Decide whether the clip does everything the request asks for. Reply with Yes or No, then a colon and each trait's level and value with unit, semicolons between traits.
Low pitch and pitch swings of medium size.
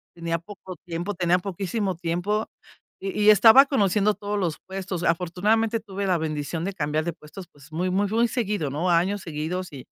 No: medium, 185 Hz; average, 3.6 semitones